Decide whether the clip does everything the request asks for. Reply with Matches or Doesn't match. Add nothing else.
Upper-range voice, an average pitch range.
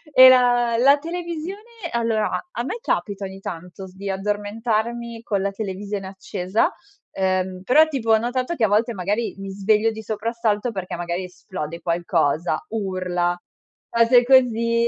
Matches